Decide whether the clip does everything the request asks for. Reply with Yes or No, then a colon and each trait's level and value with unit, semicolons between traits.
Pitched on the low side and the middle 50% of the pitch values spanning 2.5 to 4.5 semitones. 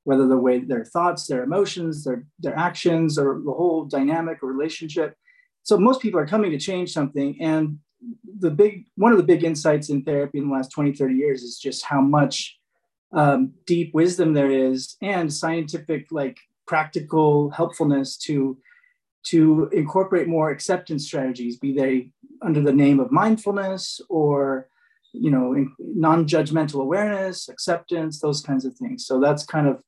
No: medium, 155 Hz; average, 4.1 semitones